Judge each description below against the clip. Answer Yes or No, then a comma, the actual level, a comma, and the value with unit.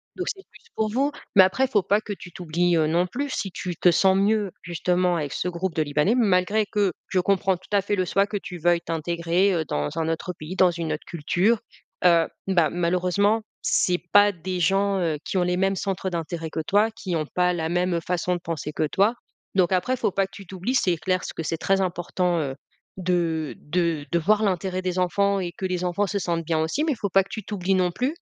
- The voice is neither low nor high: Yes, medium, 180 Hz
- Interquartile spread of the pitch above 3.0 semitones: No, narrow, 2.6 semitones